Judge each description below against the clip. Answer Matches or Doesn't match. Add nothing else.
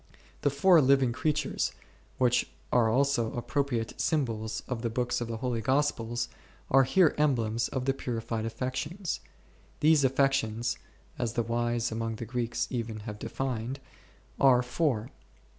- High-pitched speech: Doesn't match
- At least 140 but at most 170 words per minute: Matches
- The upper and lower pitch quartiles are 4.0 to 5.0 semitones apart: Doesn't match